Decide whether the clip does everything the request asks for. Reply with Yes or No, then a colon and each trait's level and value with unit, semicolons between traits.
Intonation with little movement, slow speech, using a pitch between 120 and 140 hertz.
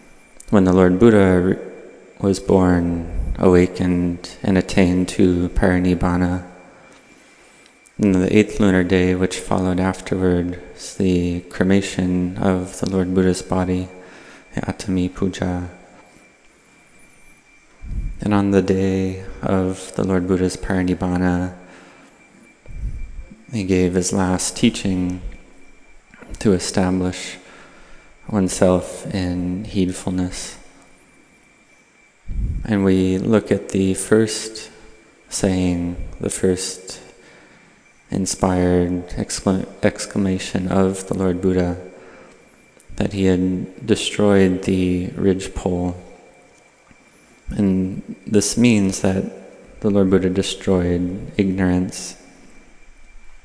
No: narrow, 1.0 semitones; slow, 90 wpm; very low, 95 Hz